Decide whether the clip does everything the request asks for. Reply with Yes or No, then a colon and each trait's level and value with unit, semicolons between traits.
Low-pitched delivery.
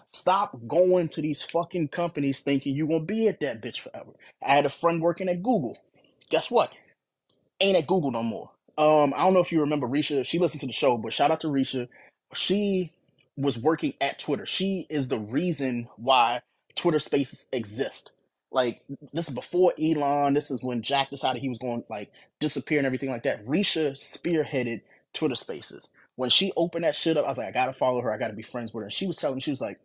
No: medium, 145 Hz